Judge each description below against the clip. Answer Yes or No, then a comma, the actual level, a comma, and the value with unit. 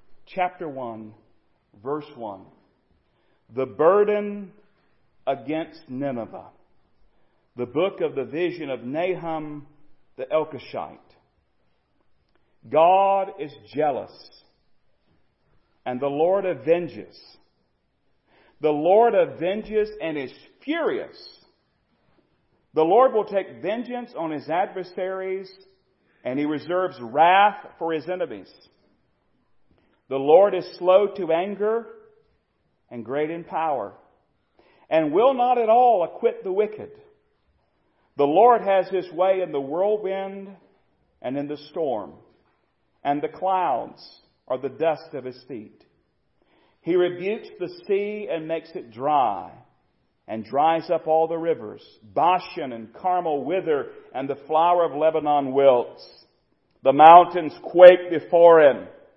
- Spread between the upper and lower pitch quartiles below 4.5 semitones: No, average, 5.0 semitones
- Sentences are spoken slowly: Yes, slow, 115 wpm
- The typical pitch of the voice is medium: Yes, medium, 175 Hz